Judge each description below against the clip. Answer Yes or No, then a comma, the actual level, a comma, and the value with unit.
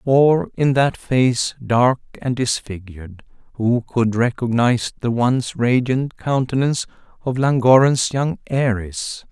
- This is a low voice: Yes, low, 125 Hz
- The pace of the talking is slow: Yes, slow, 115 wpm